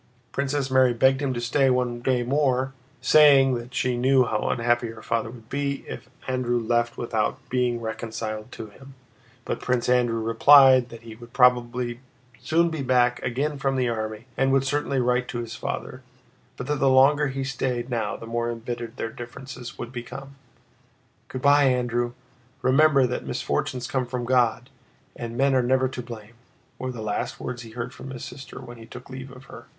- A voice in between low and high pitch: No, low, 125 Hz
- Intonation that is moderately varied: No, narrow, 2.0 semitones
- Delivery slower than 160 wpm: No, average, 185 wpm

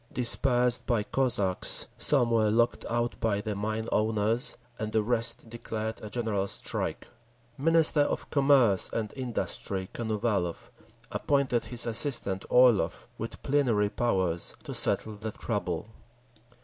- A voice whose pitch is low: Yes, low, 115 Hz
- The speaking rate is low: Yes, slow, 125 wpm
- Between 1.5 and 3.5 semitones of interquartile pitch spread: Yes, average, 2.9 semitones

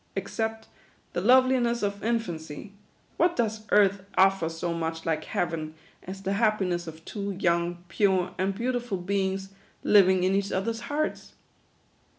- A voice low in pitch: No, high, 195 Hz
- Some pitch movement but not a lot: Yes, average, 4.0 semitones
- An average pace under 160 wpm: Yes, average, 150 wpm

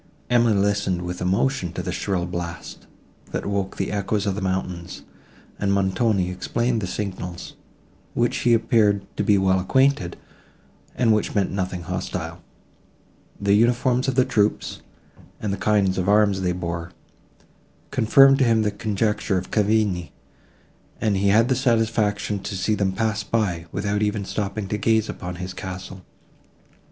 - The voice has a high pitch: No, low, 100 Hz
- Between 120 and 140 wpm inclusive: No, average, 155 wpm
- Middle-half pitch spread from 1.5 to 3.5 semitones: Yes, average, 3.0 semitones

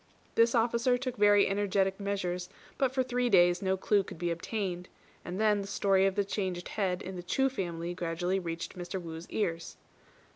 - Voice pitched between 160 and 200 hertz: Yes, high, 190 Hz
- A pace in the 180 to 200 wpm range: Yes, average, 185 wpm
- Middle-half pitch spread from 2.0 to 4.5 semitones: Yes, average, 2.9 semitones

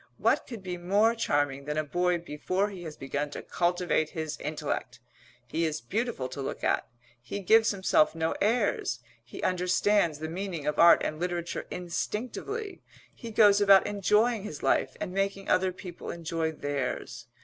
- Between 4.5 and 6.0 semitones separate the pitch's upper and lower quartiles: Yes, average, 4.8 semitones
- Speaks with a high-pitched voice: No, medium, 175 Hz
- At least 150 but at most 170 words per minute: Yes, average, 165 wpm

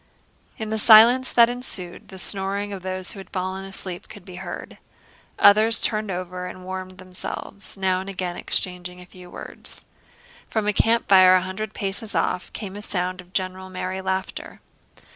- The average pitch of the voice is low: No, high, 190 Hz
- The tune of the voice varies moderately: No, narrow, 1.9 semitones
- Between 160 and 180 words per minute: Yes, average, 170 wpm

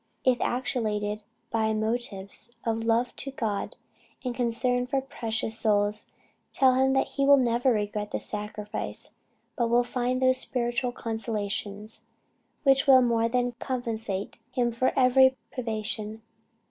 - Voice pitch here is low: No, high, 235 Hz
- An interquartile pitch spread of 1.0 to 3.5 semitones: Yes, average, 2.8 semitones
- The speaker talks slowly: Yes, slow, 130 wpm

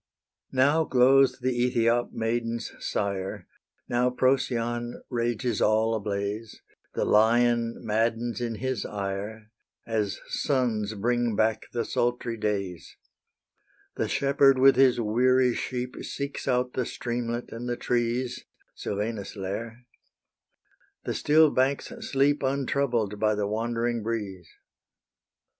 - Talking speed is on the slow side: Yes, slow, 115 wpm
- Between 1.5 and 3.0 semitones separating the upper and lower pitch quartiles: Yes, narrow, 2.6 semitones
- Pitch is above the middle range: No, low, 120 Hz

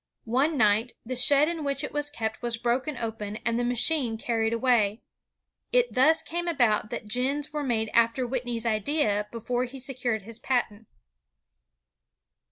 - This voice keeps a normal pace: Yes, average, 160 wpm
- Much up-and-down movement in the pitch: No, average, 3.7 semitones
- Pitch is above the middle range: Yes, high, 245 Hz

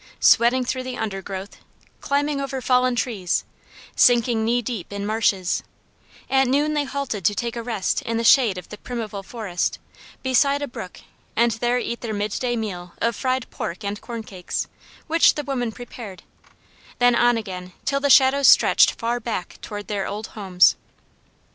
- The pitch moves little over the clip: No, average, 3.9 semitones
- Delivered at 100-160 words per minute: No, average, 170 wpm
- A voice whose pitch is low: No, high, 235 Hz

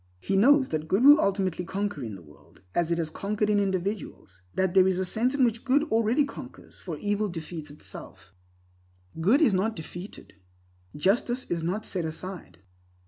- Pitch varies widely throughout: No, average, 4.8 semitones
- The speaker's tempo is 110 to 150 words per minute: No, average, 180 wpm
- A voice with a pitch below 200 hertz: Yes, high, 190 Hz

